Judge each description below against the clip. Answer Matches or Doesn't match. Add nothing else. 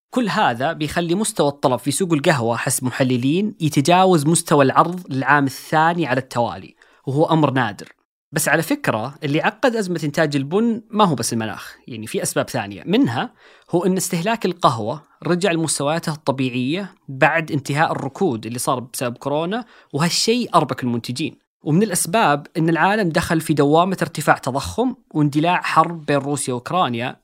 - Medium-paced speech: Doesn't match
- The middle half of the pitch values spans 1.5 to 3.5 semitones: Doesn't match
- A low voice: Doesn't match